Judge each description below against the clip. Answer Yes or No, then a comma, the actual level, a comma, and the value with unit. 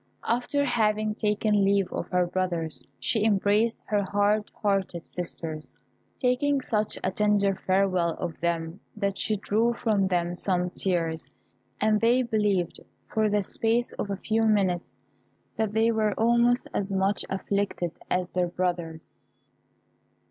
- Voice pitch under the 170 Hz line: No, high, 200 Hz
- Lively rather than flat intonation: No, average, 3.2 semitones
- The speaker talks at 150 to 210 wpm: No, average, 140 wpm